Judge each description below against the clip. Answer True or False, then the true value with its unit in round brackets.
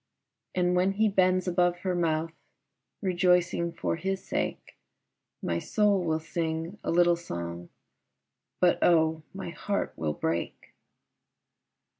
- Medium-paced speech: False (120 wpm)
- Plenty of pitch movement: False (2.4 semitones)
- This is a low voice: False (175 Hz)